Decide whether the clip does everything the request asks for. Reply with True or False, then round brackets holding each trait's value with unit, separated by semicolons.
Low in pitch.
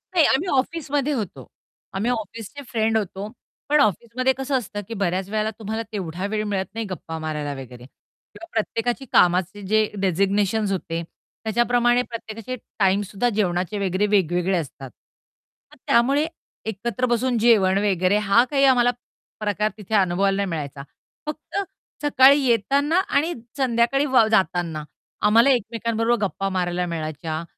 False (215 Hz)